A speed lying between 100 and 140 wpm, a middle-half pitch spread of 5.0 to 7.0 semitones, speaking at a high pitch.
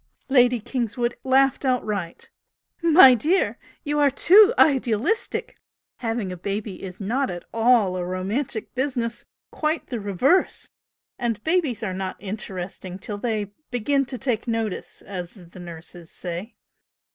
Yes: slow, 135 wpm; wide, 5.5 semitones; high, 230 Hz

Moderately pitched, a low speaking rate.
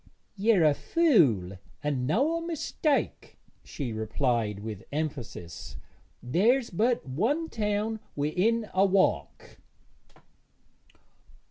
Yes: medium, 180 Hz; slow, 90 wpm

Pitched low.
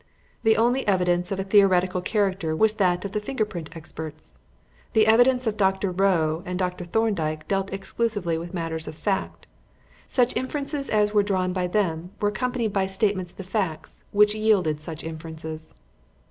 No: high, 190 Hz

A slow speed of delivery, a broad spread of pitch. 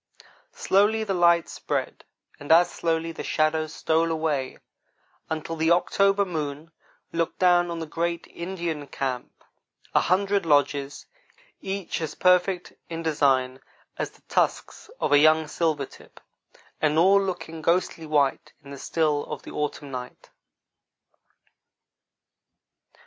No: slow, 130 wpm; average, 2.9 semitones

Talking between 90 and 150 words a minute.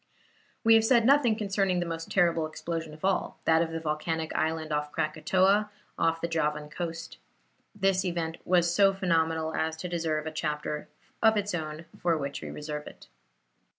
No: average, 175 wpm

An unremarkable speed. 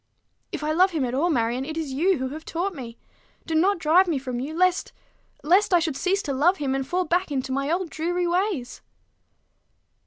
No: fast, 215 wpm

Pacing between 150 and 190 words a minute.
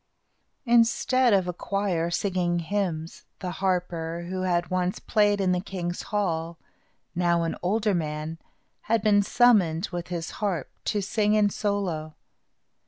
No: average, 140 wpm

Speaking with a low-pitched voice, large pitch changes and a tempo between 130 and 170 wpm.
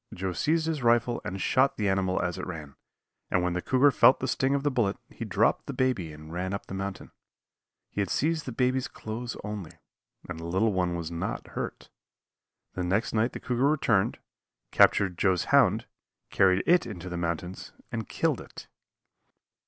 No: low, 100 Hz; wide, 5.9 semitones; average, 185 wpm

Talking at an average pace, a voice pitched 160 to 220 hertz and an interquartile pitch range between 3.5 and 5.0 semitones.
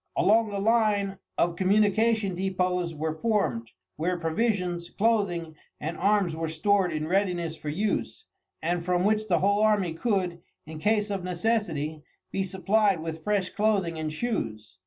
Yes: average, 150 wpm; medium, 185 Hz; average, 4.0 semitones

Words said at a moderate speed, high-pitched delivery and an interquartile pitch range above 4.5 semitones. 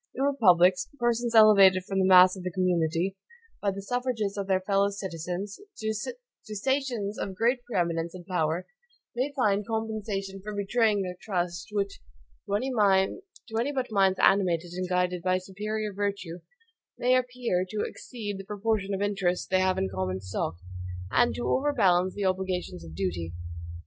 No: average, 160 wpm; high, 195 Hz; average, 3.3 semitones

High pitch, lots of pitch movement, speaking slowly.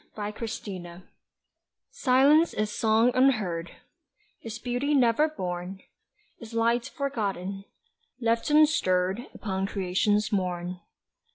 No: high, 215 Hz; average, 4.7 semitones; slow, 90 wpm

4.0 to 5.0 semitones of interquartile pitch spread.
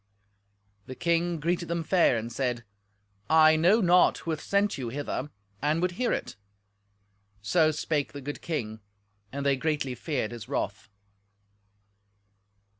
Yes: average, 4.6 semitones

